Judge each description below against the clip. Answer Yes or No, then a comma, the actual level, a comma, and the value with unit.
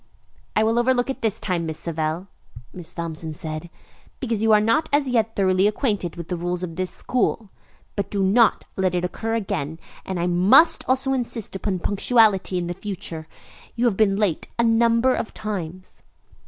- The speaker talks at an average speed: Yes, average, 180 wpm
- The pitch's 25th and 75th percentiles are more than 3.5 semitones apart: Yes, average, 4.5 semitones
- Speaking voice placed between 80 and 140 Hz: No, high, 195 Hz